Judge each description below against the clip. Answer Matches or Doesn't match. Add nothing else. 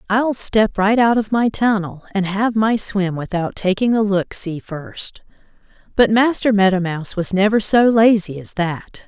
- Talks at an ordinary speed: Matches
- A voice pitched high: Matches